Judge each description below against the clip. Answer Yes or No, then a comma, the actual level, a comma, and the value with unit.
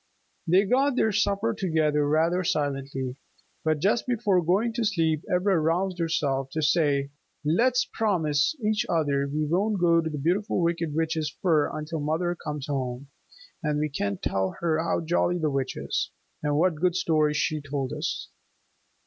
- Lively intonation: No, average, 3.7 semitones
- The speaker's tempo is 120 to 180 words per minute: Yes, average, 165 wpm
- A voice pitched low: No, medium, 160 Hz